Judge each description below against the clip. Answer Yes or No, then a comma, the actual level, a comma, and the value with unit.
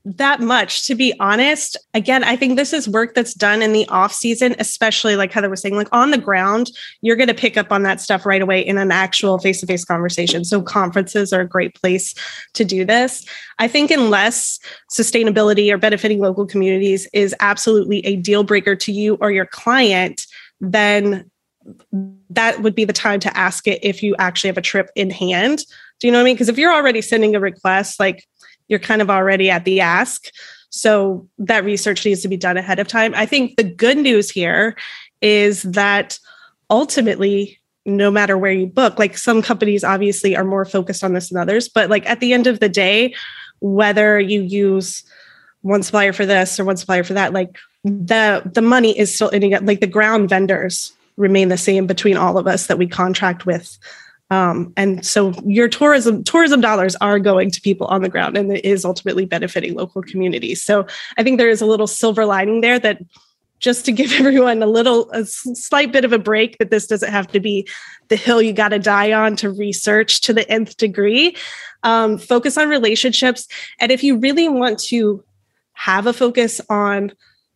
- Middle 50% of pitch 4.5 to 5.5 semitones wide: No, average, 3.0 semitones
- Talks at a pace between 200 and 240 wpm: Yes, fast, 205 wpm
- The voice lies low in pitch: No, high, 205 Hz